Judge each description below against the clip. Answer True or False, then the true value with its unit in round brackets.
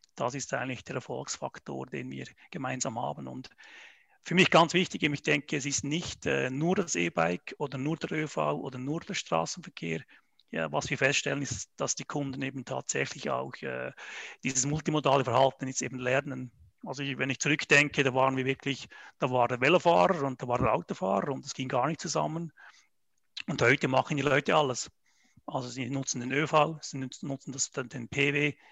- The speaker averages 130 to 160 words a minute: False (190 wpm)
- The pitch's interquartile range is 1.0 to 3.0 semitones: True (2.5 semitones)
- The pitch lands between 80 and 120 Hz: False (135 Hz)